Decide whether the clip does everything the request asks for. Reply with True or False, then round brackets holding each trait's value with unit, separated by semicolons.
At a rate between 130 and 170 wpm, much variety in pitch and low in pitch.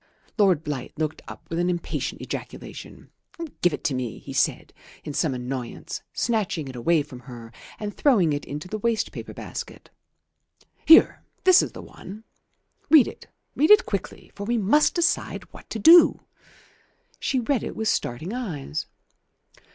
False (160 wpm; 8.4 semitones; 180 Hz)